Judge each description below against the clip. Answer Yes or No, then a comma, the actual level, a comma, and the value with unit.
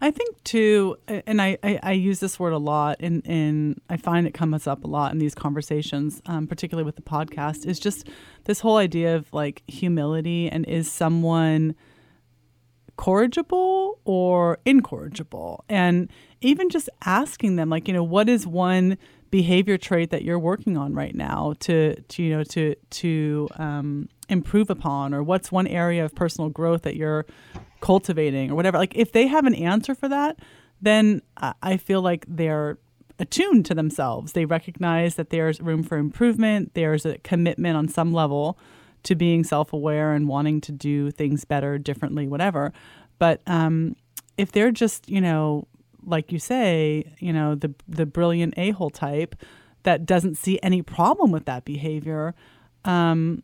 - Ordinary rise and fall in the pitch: Yes, average, 3.8 semitones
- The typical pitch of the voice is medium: Yes, medium, 165 Hz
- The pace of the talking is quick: No, average, 170 wpm